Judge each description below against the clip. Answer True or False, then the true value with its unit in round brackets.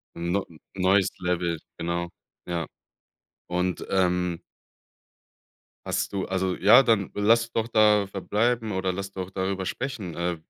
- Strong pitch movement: False (2.8 semitones)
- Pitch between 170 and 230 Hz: False (95 Hz)